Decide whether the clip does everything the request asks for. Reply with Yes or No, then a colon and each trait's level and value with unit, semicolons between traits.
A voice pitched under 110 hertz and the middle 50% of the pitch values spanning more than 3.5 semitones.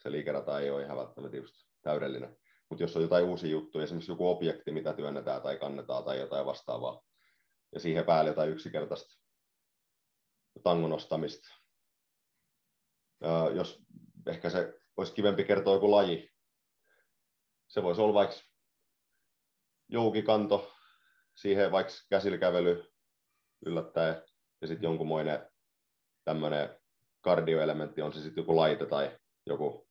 Yes: very low, 80 Hz; average, 4.1 semitones